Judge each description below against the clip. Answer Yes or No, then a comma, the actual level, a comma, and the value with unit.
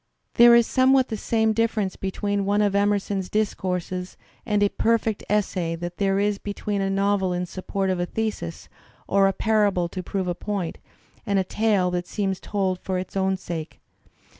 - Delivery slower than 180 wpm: No, average, 185 wpm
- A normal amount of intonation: No, narrow, 2.1 semitones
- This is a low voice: No, high, 195 Hz